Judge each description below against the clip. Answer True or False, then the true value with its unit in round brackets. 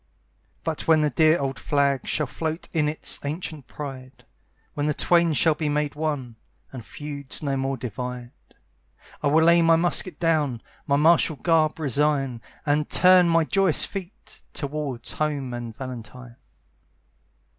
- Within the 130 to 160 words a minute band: True (145 wpm)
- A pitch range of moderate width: True (3.3 semitones)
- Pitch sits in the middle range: True (150 Hz)